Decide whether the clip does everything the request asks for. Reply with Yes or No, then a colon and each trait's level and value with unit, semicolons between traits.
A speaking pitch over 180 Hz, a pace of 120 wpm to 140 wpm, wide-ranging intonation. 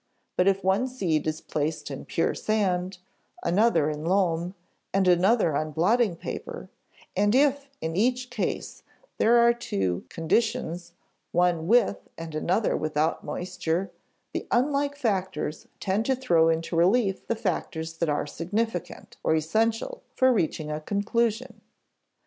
Yes: high, 190 Hz; slow, 135 wpm; wide, 6.1 semitones